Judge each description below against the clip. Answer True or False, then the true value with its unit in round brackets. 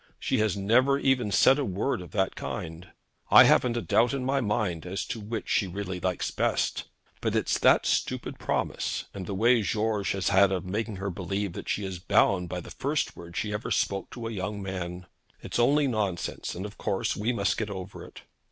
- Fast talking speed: True (215 wpm)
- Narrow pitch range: False (3.4 semitones)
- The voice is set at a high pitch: False (100 Hz)